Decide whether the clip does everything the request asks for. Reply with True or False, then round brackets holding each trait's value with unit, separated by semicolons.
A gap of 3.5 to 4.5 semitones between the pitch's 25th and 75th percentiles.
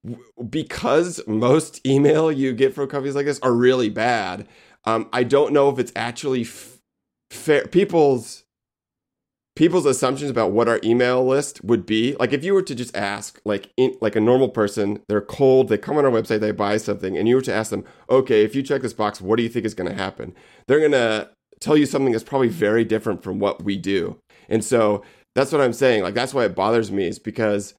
True (4.0 semitones)